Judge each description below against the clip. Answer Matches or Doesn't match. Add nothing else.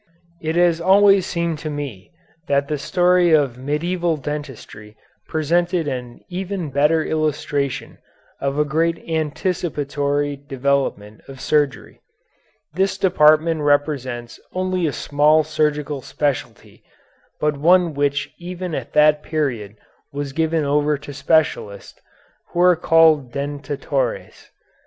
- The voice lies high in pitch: Doesn't match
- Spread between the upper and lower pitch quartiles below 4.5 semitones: Matches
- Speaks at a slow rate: Matches